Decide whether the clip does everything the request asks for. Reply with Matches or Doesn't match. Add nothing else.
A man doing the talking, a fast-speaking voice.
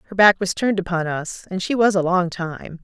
Doesn't match